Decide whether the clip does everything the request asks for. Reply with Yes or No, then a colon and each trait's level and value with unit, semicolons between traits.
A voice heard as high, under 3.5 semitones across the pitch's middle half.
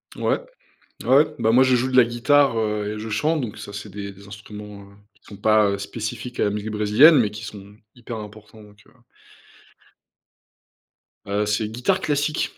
No: low, 105 Hz; average, 3.0 semitones